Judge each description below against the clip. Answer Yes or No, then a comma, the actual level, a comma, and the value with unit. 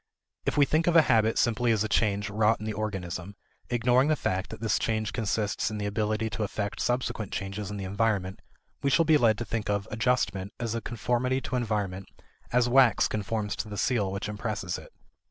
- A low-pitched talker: Yes, low, 110 Hz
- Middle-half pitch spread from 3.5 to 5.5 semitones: No, average, 2.7 semitones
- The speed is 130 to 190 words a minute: No, fast, 205 wpm